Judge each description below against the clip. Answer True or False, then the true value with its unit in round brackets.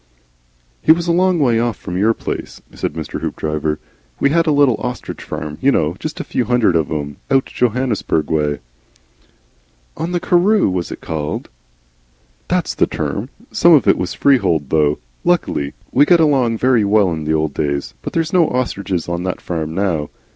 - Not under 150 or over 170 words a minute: False (185 wpm)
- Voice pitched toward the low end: True (105 Hz)